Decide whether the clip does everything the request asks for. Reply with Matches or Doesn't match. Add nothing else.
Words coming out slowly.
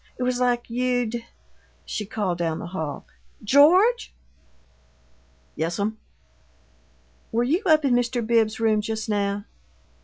Matches